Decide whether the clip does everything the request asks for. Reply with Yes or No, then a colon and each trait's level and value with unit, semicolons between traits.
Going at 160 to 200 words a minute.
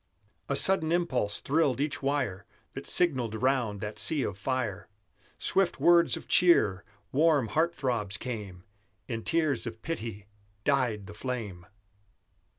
No: slow, 135 wpm